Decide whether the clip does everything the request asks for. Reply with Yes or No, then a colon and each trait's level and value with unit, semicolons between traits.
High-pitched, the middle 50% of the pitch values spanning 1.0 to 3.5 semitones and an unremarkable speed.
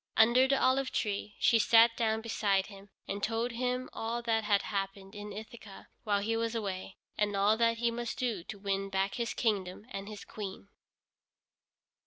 Yes: high, 220 Hz; average, 2.7 semitones; average, 180 wpm